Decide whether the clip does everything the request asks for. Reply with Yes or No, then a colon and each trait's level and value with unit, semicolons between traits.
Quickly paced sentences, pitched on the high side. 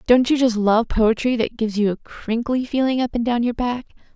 Yes: fast, 230 wpm; high, 235 Hz